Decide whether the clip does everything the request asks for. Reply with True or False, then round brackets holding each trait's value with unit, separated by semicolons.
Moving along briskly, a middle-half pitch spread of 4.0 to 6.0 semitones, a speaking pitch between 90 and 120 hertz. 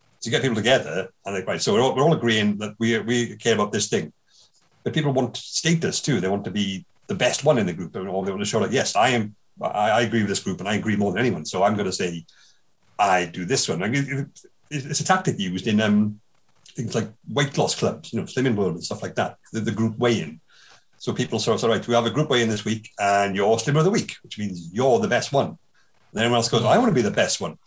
True (280 wpm; 5.1 semitones; 115 Hz)